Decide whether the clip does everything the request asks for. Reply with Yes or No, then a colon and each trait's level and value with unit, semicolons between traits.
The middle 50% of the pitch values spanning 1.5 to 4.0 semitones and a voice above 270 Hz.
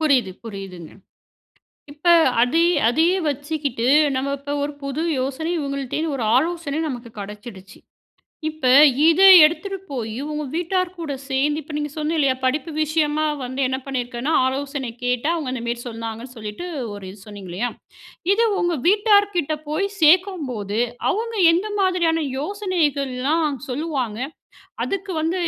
No: average, 4.8 semitones; very high, 285 Hz